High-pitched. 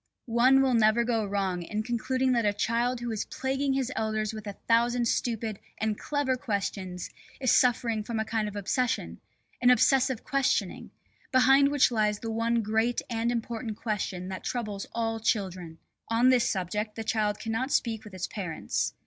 Yes: high, 225 Hz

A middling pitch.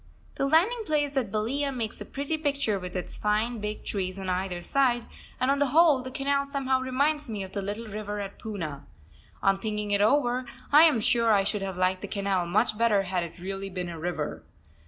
No: high, 215 Hz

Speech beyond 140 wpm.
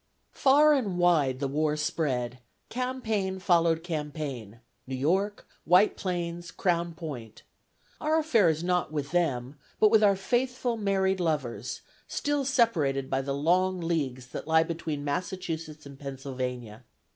No: slow, 135 wpm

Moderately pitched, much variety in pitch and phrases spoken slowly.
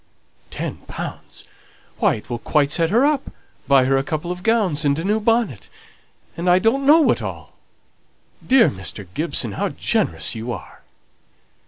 No: medium, 165 Hz; wide, 8.9 semitones; average, 165 wpm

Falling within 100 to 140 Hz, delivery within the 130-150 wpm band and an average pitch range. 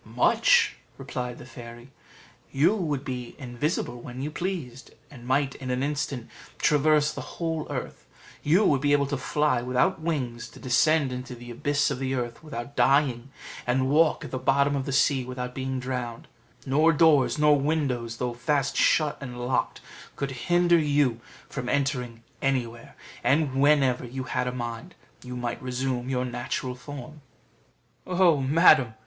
No: low, 135 Hz; average, 160 wpm; average, 3.1 semitones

